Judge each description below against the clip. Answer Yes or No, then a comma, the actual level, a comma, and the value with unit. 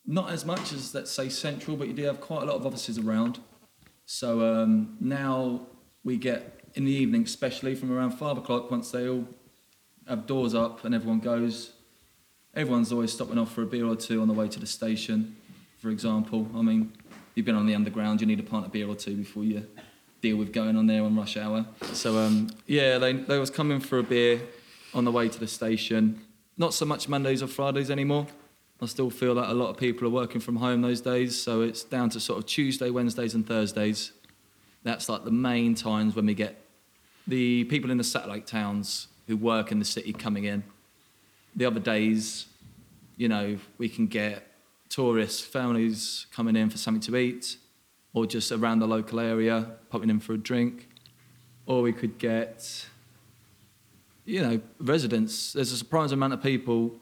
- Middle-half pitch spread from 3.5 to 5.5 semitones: No, narrow, 2.6 semitones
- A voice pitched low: Yes, low, 115 Hz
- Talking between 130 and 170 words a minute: No, average, 200 wpm